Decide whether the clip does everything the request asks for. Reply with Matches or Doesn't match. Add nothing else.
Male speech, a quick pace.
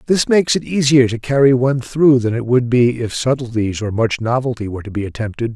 Matches